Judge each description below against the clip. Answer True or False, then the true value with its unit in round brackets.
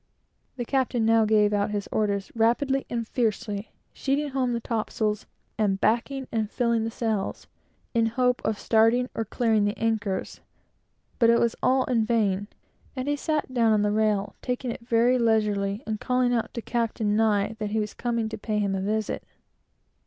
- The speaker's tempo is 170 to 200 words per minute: True (180 wpm)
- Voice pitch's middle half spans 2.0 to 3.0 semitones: True (2.5 semitones)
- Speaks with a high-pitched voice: True (225 Hz)